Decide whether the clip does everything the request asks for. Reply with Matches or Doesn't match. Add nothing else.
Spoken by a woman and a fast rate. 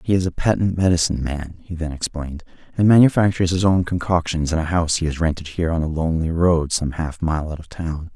Doesn't match